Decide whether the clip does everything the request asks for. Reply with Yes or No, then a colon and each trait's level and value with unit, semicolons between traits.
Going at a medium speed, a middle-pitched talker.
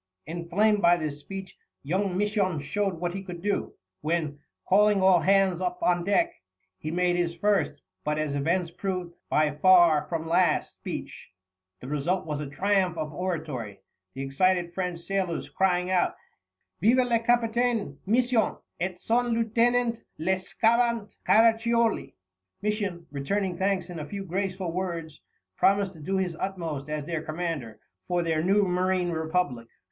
Yes: average, 150 wpm; medium, 180 Hz